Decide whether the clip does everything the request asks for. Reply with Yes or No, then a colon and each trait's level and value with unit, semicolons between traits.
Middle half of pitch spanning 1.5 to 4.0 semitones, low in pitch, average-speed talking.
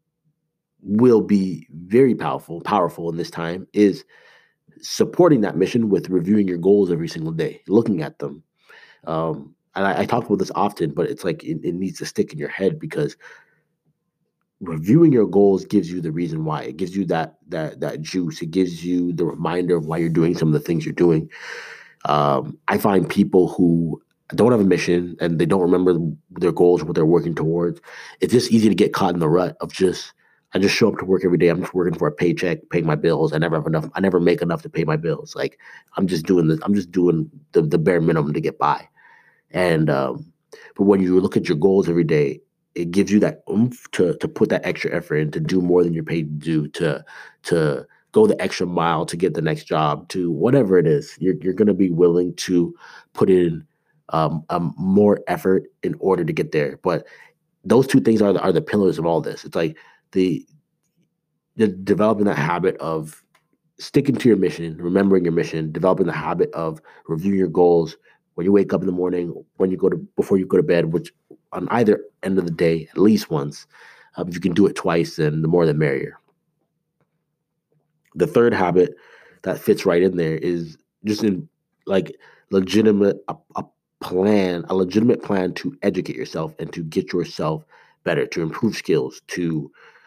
No: average, 3.4 semitones; very low, 90 Hz; fast, 210 wpm